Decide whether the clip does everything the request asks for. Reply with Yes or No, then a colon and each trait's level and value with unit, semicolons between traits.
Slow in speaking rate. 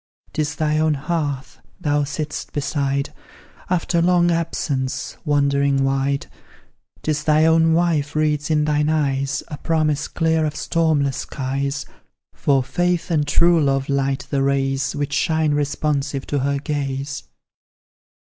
Yes: slow, 130 wpm